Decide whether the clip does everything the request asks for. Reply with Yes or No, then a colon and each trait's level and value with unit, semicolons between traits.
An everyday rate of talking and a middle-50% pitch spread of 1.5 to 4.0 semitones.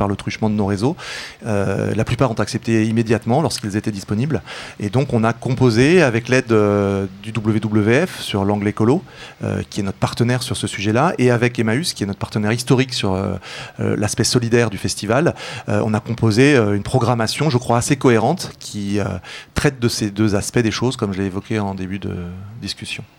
Yes: average, 200 wpm; average, 3.1 semitones